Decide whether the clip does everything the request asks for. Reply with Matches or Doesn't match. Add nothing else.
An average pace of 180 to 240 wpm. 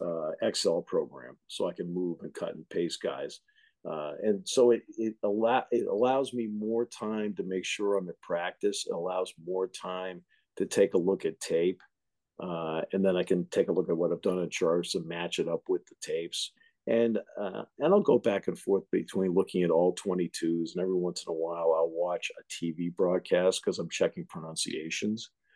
Matches